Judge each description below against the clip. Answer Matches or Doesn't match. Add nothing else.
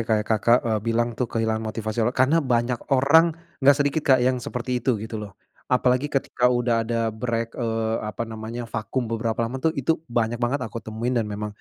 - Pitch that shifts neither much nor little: Doesn't match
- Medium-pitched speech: Doesn't match